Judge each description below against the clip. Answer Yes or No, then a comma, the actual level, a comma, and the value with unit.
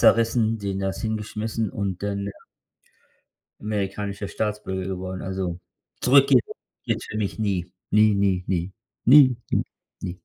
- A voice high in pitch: No, low, 100 Hz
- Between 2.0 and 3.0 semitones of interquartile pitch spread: Yes, narrow, 2.5 semitones